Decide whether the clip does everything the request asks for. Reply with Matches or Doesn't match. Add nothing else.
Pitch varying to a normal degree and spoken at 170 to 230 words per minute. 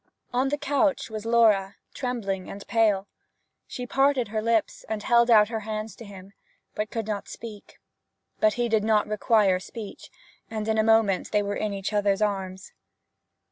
Doesn't match